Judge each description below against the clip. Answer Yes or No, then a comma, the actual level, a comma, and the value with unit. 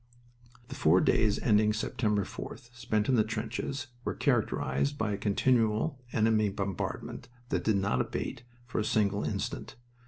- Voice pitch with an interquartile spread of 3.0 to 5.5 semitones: No, narrow, 2.5 semitones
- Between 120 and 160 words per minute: Yes, average, 150 wpm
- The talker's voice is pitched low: Yes, low, 110 Hz